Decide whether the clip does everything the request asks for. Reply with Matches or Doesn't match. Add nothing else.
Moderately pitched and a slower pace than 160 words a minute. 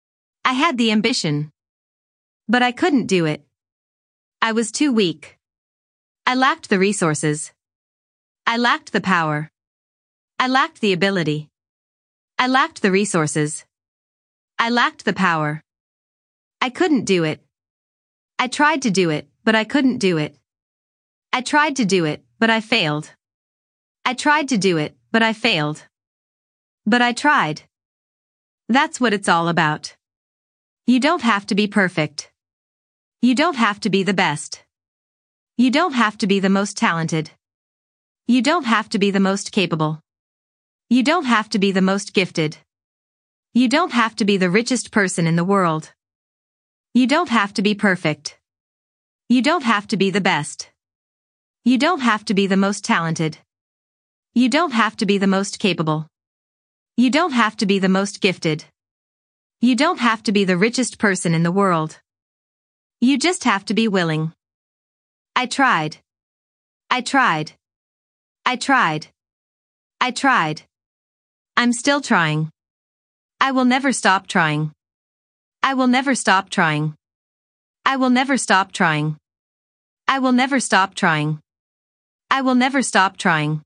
Matches